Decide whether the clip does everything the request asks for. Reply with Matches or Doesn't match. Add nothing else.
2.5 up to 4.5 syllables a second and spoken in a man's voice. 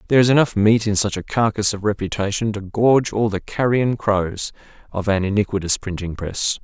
Doesn't match